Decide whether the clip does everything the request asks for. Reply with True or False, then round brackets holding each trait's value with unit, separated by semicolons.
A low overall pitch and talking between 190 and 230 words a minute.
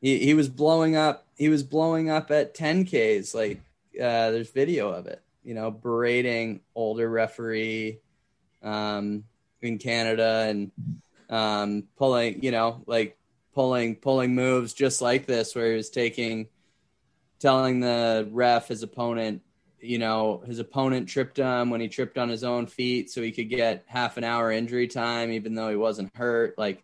False (120 Hz; 165 wpm)